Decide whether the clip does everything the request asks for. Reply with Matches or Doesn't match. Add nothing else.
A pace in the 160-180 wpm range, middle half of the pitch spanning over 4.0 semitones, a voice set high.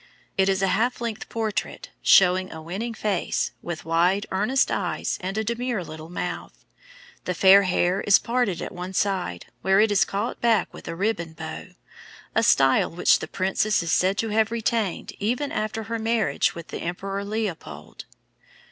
Doesn't match